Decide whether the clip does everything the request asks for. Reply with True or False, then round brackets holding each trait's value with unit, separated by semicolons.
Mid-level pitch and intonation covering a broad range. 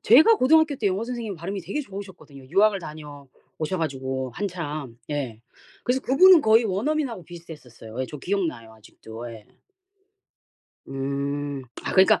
True (165 Hz; 7.9 semitones)